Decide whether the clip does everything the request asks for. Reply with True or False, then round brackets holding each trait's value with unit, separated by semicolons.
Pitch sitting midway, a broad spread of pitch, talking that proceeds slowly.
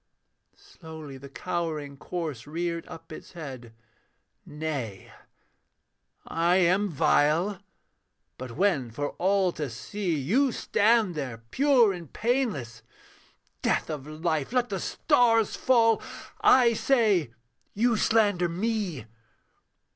True (170 Hz; 6.7 semitones; 110 wpm)